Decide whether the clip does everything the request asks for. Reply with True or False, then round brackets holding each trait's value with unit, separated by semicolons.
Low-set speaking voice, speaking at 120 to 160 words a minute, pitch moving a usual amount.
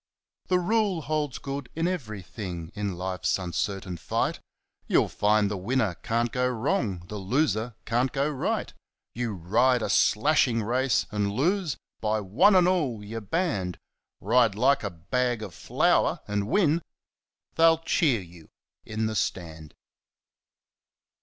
False (115 Hz; 140 wpm; 5.9 semitones)